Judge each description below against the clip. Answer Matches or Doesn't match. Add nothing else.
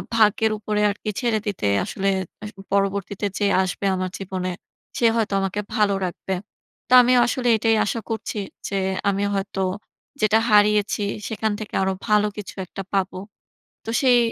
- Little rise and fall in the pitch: Matches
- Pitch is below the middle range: Doesn't match